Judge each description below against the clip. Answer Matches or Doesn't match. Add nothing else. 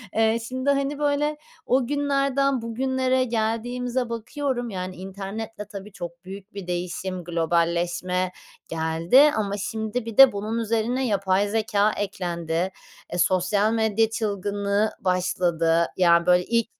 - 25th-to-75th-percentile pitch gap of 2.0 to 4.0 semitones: Doesn't match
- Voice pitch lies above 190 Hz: Matches